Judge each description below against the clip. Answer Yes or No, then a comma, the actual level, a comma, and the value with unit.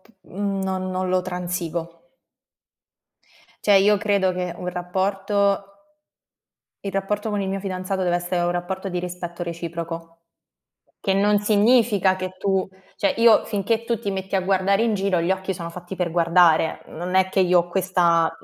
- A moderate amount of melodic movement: No, narrow, 2.1 semitones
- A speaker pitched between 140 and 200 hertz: Yes, medium, 185 Hz